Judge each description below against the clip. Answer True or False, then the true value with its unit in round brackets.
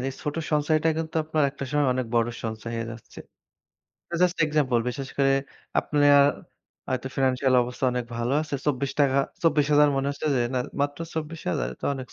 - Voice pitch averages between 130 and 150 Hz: True (140 Hz)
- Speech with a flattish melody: False (3.0 semitones)